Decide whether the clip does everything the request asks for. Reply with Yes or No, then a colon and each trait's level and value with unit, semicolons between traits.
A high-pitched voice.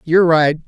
No: medium, 165 Hz